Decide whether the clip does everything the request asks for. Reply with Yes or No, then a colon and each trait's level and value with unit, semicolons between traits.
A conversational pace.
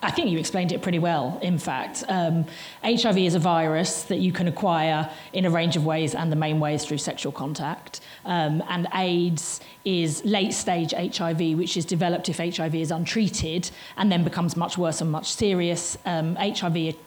Yes: average, 190 wpm